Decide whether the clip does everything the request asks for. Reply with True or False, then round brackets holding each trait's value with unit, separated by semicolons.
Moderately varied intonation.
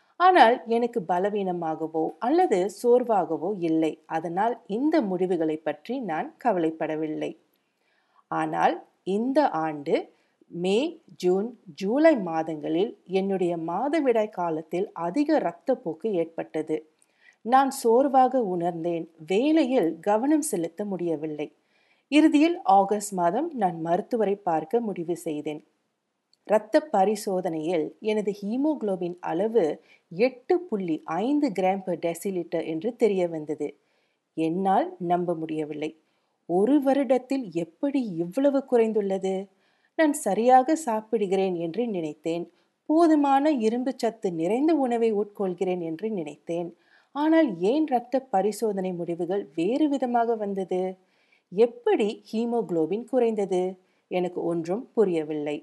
False (6.4 semitones)